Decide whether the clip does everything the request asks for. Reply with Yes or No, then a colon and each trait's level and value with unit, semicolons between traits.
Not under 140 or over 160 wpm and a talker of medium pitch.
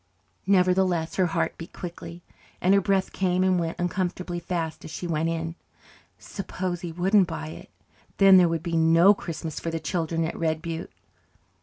No: average, 175 wpm; medium, 175 Hz